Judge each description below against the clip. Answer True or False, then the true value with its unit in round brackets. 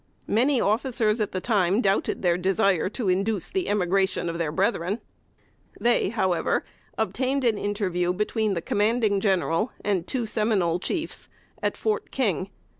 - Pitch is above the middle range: True (205 Hz)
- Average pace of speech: True (145 wpm)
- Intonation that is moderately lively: True (3.8 semitones)